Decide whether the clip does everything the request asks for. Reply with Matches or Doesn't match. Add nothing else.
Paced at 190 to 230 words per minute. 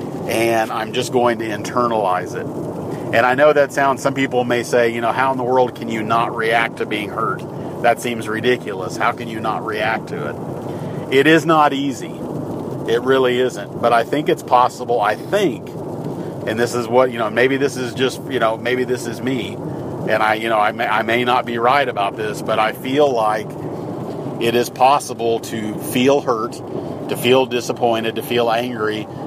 Matches